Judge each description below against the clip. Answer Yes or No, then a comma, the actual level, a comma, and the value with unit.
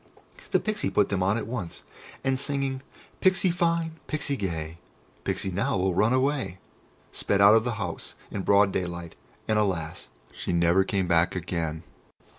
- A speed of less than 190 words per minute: Yes, average, 160 wpm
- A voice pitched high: No, low, 100 Hz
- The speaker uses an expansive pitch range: Yes, wide, 6.9 semitones